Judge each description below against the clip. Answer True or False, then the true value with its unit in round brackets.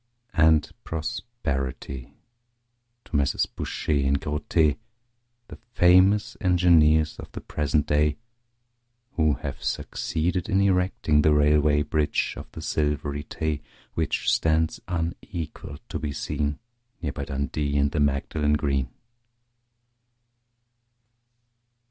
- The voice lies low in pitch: True (75 Hz)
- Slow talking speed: True (105 wpm)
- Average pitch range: False (2.2 semitones)